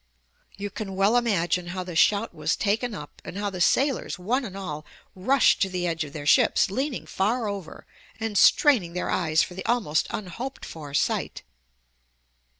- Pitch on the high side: Yes, high, 195 Hz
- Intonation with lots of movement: No, average, 4.5 semitones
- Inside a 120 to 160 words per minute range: No, average, 175 wpm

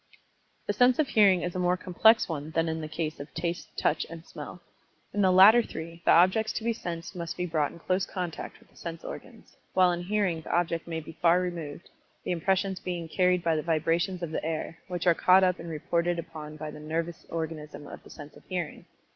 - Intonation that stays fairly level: Yes, narrow, 2.1 semitones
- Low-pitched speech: No, medium, 170 Hz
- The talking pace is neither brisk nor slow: No, fast, 225 wpm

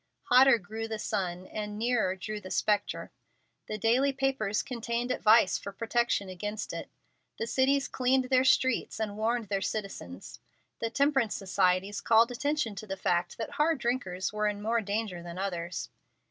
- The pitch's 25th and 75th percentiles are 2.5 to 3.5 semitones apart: No, average, 4.0 semitones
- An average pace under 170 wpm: Yes, average, 160 wpm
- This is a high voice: Yes, high, 215 Hz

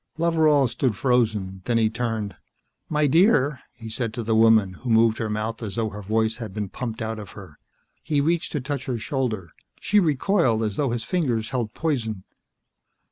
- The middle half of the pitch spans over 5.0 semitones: No, average, 4.1 semitones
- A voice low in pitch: Yes, low, 115 Hz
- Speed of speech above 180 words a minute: Yes, average, 190 wpm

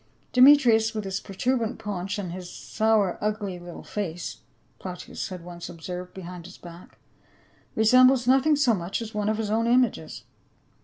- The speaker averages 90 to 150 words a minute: No, average, 185 wpm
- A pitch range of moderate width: Yes, average, 4.3 semitones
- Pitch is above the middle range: Yes, high, 210 Hz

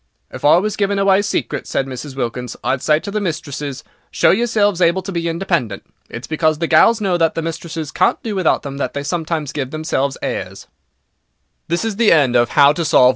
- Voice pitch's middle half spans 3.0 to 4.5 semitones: No, average, 5.2 semitones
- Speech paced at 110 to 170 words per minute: No, average, 195 wpm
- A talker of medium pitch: Yes, medium, 165 Hz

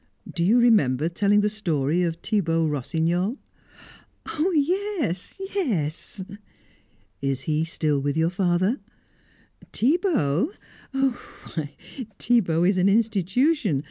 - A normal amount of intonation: No, wide, 7.1 semitones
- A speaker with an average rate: No, slow, 105 wpm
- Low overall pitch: No, medium, 185 Hz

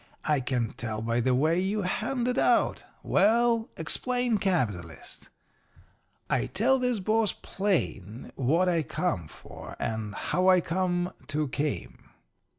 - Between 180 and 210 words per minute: No, slow, 135 wpm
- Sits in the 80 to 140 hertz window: No, medium, 175 Hz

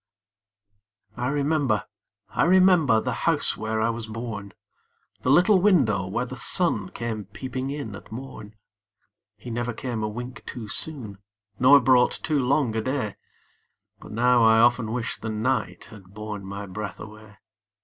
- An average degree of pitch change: Yes, average, 3.5 semitones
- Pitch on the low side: Yes, low, 115 Hz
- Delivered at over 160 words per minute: No, average, 155 wpm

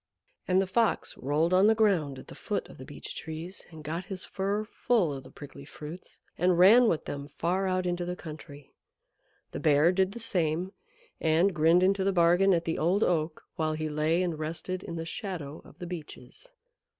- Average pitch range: Yes, average, 3.2 semitones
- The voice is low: No, medium, 175 Hz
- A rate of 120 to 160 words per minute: No, average, 200 wpm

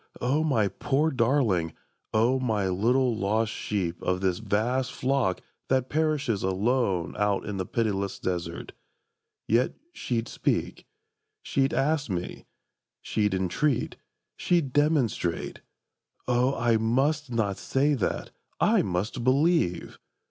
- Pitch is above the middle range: No, low, 115 Hz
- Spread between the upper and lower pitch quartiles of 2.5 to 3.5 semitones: No, wide, 5.4 semitones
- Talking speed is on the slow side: Yes, slow, 115 wpm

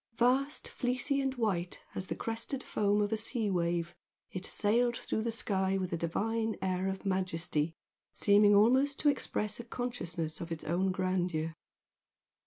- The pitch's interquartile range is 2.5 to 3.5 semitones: No, average, 4.5 semitones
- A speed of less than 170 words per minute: Yes, average, 160 wpm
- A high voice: Yes, high, 205 Hz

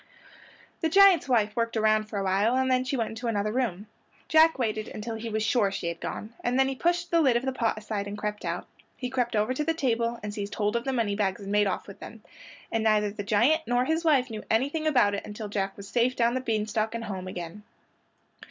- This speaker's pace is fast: Yes, fast, 245 wpm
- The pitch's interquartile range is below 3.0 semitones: No, average, 3.6 semitones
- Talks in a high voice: Yes, high, 225 Hz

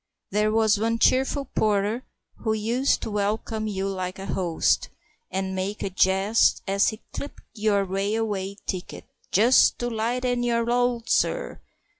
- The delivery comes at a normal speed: Yes, average, 145 wpm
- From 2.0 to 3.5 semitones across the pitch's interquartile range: Yes, average, 3.0 semitones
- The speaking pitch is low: No, high, 215 Hz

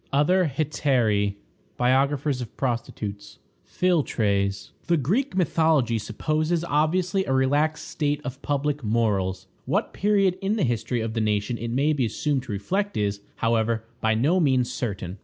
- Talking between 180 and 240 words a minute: No, average, 145 wpm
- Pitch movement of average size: No, wide, 6.0 semitones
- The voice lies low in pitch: Yes, low, 130 Hz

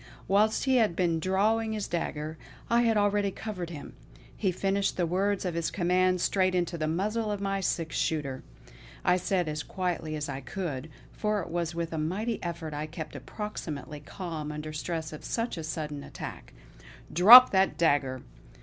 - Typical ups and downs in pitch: Yes, average, 4.3 semitones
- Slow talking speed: No, average, 175 wpm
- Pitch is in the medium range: Yes, medium, 175 Hz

